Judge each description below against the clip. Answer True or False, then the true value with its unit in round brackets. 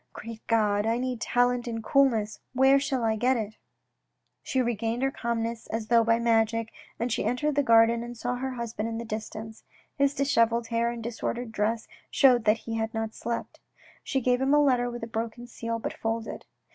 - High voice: True (230 Hz)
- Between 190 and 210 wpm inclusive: True (200 wpm)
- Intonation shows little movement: True (1.7 semitones)